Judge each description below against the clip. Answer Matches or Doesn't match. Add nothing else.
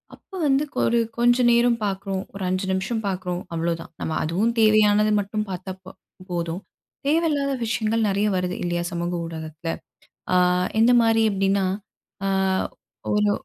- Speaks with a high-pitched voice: Matches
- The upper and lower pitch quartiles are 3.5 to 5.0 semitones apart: Matches